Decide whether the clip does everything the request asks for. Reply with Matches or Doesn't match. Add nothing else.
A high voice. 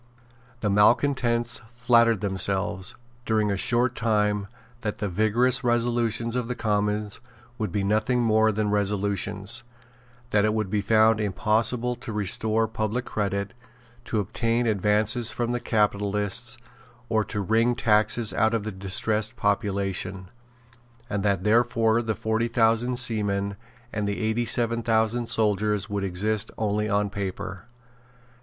Doesn't match